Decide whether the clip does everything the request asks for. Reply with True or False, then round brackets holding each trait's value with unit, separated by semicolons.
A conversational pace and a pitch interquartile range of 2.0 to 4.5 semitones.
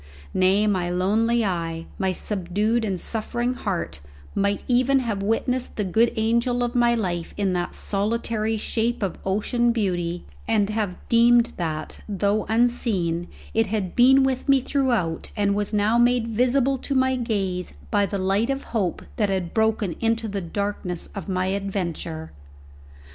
True (155 wpm; 4.0 semitones)